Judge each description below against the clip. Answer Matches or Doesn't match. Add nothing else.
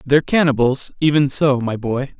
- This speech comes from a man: Matches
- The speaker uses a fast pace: Doesn't match